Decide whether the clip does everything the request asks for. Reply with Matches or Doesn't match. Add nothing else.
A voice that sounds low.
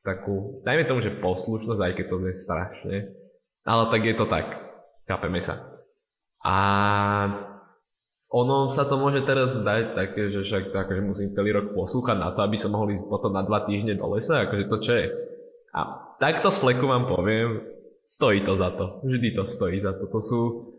Matches